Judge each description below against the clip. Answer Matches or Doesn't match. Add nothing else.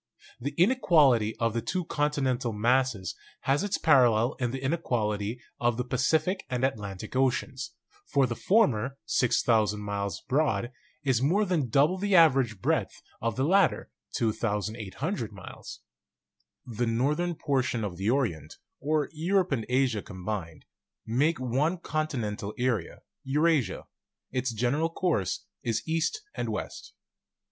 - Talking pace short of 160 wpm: Matches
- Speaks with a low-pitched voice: Matches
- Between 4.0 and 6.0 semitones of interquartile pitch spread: Matches